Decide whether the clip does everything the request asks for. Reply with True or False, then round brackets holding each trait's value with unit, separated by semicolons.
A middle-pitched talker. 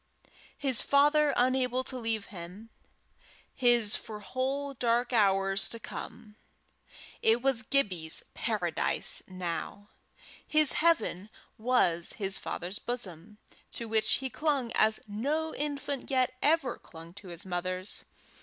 False (225 Hz)